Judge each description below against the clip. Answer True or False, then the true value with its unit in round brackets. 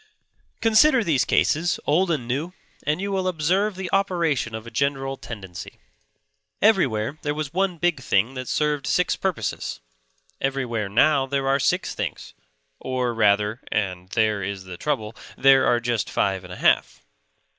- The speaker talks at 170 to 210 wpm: False (160 wpm)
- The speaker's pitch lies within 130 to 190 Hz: True (135 Hz)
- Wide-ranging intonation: True (7.3 semitones)